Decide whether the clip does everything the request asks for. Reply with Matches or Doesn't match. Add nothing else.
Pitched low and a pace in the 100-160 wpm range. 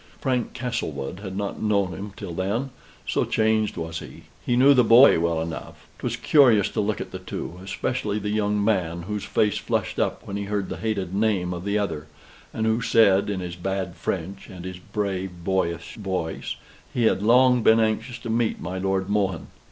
Doesn't match